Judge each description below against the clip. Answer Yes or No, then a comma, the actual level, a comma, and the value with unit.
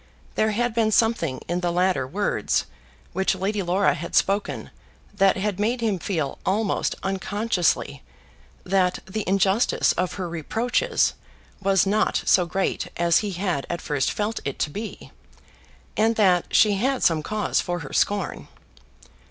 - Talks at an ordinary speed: Yes, average, 150 wpm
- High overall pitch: Yes, high, 195 Hz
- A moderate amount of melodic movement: Yes, average, 3.3 semitones